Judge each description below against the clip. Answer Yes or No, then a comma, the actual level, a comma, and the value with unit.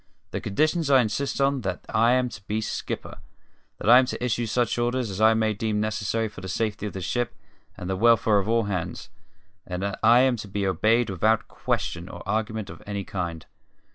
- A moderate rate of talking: No, fast, 215 wpm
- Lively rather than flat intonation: No, average, 3.2 semitones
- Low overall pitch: Yes, low, 110 Hz